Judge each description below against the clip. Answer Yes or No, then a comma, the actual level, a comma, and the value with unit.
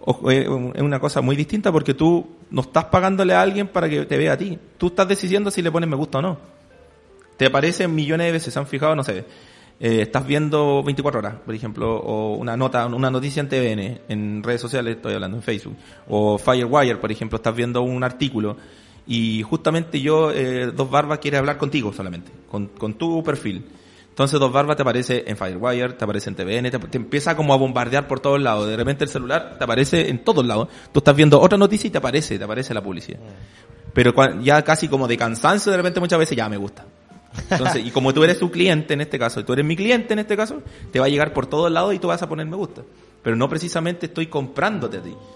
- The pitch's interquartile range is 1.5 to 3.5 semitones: No, wide, 5.4 semitones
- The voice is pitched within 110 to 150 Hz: Yes, medium, 140 Hz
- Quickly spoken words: Yes, fast, 230 wpm